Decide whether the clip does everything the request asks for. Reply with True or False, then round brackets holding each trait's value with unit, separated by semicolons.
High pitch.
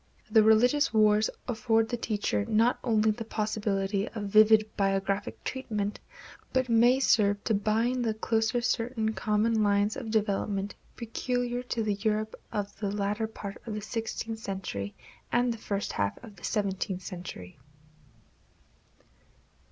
True (215 Hz)